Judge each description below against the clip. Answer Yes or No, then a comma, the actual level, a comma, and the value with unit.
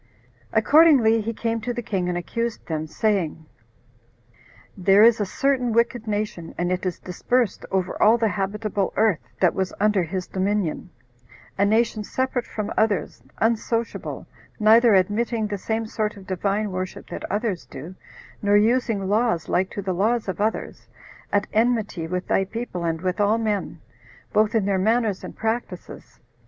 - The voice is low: No, high, 210 Hz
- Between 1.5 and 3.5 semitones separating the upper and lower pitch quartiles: Yes, average, 3.2 semitones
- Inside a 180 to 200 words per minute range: No, average, 160 wpm